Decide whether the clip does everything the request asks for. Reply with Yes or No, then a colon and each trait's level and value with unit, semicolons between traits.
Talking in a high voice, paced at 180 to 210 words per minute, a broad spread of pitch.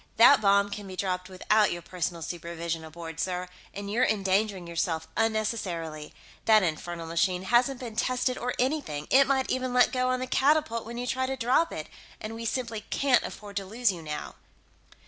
Yes: high, 210 Hz; average, 185 wpm; wide, 6.2 semitones